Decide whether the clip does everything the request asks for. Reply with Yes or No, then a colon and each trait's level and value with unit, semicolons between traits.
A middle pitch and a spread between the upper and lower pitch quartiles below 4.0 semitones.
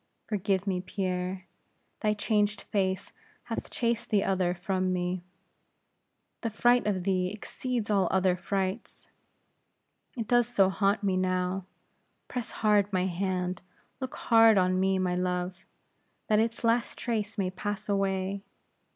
No: high, 195 Hz; narrow, 2.4 semitones